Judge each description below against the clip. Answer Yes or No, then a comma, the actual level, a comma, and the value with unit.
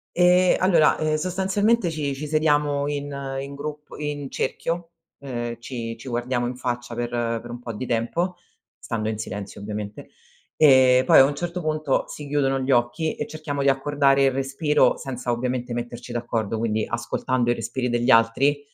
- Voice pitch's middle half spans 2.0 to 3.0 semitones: No, average, 3.8 semitones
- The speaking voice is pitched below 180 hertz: Yes, low, 135 Hz